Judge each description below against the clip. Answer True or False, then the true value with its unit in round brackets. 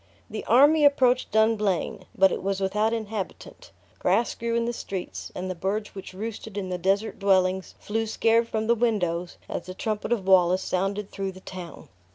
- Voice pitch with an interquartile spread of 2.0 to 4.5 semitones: True (3.2 semitones)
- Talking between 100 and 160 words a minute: False (185 wpm)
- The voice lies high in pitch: True (205 Hz)